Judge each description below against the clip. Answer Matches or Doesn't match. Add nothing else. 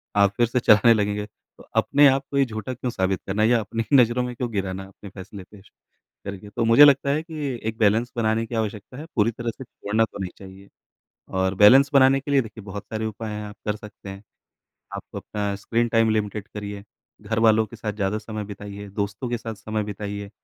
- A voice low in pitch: Matches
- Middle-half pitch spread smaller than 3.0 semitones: Matches